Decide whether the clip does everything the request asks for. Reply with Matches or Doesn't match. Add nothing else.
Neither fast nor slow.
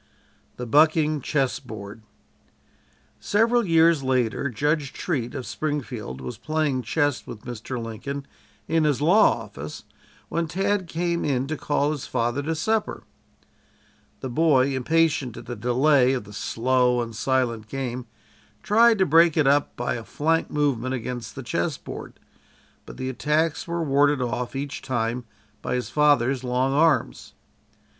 Matches